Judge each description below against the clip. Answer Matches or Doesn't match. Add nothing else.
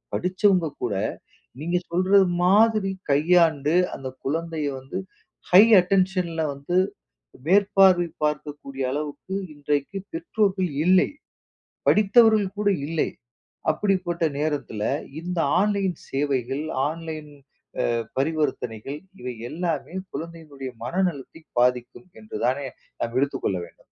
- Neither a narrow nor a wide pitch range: Matches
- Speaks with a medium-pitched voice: Matches